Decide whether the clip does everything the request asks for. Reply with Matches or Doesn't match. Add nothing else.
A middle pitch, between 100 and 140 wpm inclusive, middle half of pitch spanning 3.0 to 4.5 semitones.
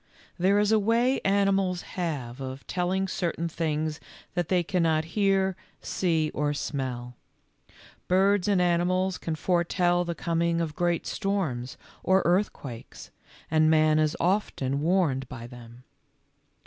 Matches